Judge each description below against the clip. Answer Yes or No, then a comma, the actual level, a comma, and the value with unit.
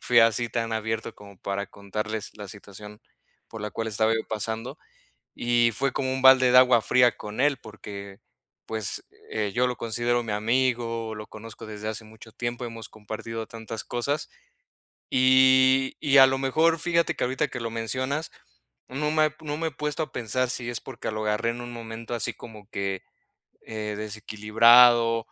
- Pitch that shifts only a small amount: No, average, 3.0 semitones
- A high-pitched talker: No, low, 115 Hz